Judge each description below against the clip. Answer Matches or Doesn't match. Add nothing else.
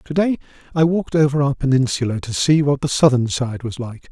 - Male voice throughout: Matches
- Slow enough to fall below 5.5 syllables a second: Doesn't match